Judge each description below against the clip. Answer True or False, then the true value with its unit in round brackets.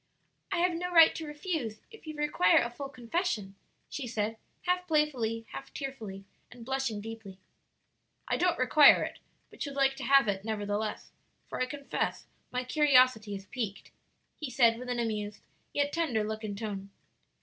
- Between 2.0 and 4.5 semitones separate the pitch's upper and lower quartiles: False (5.4 semitones)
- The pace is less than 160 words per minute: False (170 wpm)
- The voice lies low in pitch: False (250 Hz)